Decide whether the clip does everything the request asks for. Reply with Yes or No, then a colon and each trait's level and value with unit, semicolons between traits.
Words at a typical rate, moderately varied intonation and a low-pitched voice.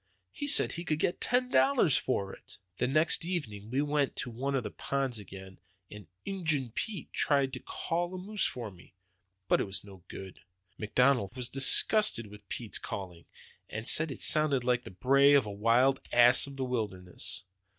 No: average, 180 wpm; wide, 6.5 semitones; low, 130 Hz